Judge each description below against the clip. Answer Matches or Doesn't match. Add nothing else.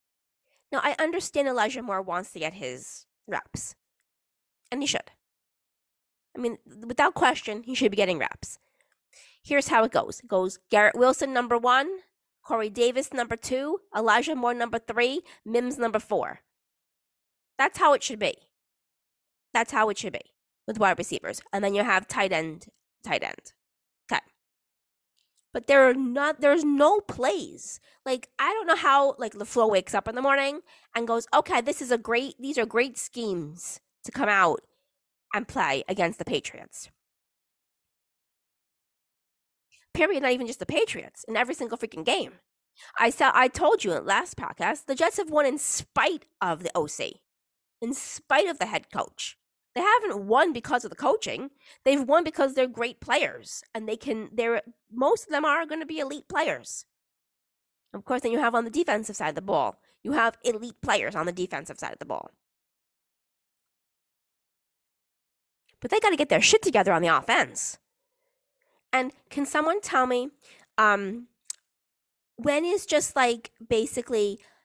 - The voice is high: Matches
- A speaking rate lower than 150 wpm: Doesn't match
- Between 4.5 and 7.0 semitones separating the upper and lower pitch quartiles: Matches